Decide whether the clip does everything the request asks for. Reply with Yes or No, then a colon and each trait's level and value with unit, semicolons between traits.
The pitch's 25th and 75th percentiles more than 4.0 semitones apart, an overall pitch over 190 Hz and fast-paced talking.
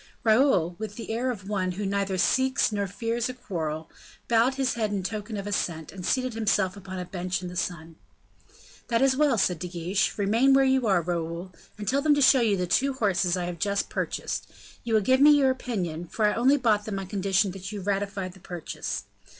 Yes: average, 4.7 semitones; high, 205 Hz; fast, 220 wpm